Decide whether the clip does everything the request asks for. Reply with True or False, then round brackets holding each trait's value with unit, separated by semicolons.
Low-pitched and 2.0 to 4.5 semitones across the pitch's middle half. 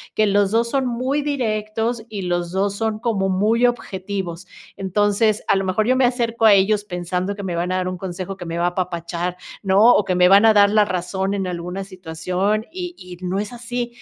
False (200 Hz; 3.4 semitones)